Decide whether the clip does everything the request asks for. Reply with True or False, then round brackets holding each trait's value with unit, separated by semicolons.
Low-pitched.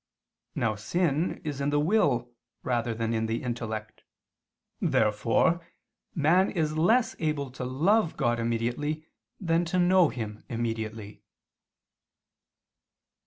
True (130 Hz)